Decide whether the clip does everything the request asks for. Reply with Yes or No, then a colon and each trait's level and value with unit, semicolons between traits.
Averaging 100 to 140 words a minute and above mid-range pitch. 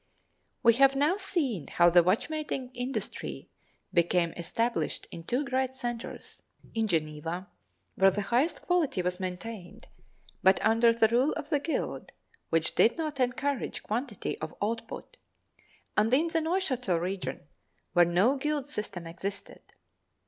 Yes: slow, 135 wpm; high, 230 Hz